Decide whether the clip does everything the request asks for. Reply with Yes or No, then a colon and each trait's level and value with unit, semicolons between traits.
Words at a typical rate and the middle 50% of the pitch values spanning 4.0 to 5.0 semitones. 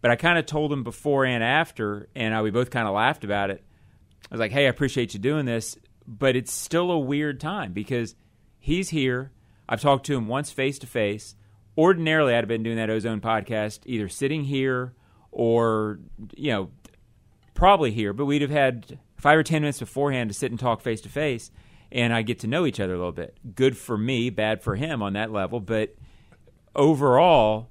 No: fast, 210 wpm; average, 4.4 semitones